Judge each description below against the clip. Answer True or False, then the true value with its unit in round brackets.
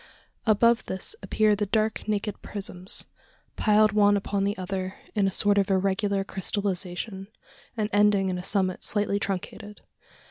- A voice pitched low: False (200 Hz)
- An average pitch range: False (1.5 semitones)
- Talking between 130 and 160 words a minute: True (145 wpm)